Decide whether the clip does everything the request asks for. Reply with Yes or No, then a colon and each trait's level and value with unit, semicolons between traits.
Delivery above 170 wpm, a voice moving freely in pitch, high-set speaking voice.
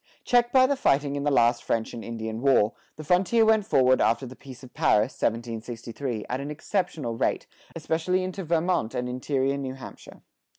No: average, 180 wpm; wide, 6.2 semitones; low, 135 Hz